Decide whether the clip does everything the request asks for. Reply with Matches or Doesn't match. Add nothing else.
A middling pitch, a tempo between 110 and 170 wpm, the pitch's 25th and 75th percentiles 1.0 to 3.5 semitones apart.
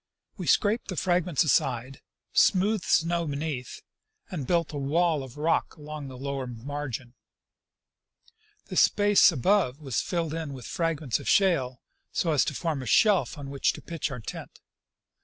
Doesn't match